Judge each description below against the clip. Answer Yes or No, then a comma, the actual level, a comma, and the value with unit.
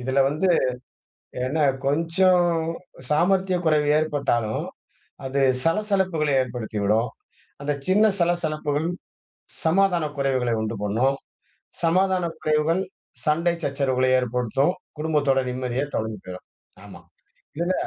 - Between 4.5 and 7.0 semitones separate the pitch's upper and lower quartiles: Yes, average, 5.0 semitones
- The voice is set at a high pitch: No, medium, 150 Hz